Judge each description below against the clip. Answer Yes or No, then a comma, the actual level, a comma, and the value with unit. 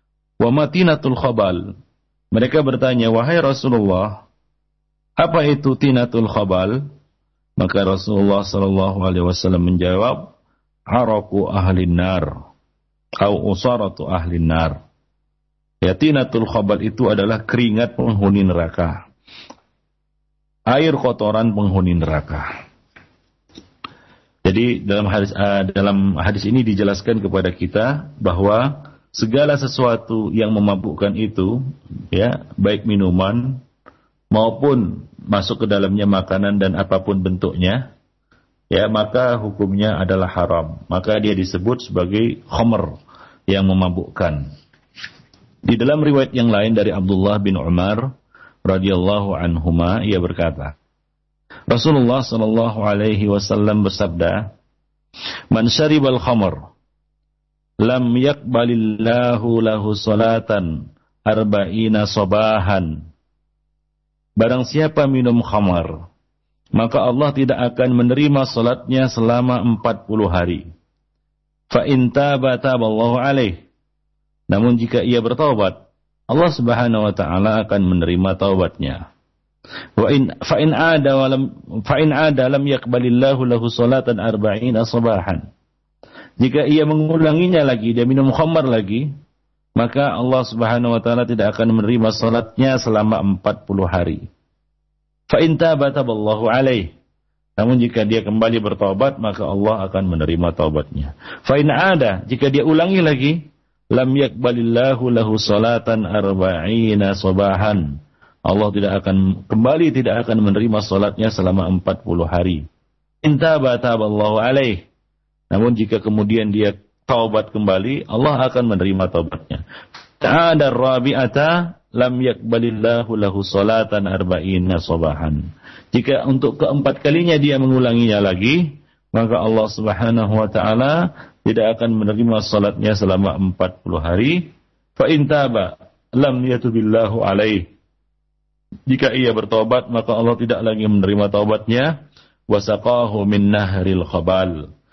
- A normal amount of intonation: Yes, average, 4.6 semitones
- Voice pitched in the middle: No, low, 110 Hz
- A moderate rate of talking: No, slow, 110 wpm